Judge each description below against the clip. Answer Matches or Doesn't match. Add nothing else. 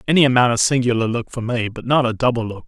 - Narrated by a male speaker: Matches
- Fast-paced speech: Matches